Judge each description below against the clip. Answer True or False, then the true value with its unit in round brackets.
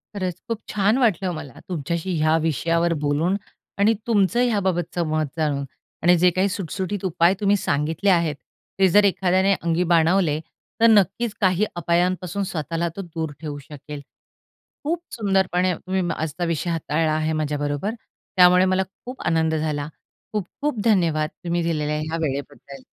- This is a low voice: False (175 Hz)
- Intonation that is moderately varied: True (3.6 semitones)